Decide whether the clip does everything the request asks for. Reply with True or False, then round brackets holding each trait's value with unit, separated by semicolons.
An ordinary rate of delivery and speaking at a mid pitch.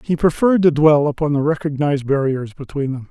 True (195 wpm; 145 Hz)